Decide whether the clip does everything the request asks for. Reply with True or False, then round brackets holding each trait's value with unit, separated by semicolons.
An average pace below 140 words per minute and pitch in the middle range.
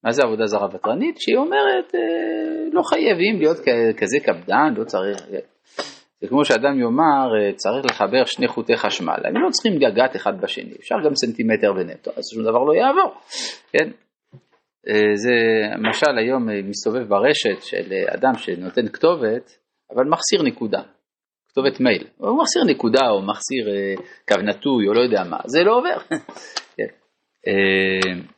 False (150 wpm; 155 Hz)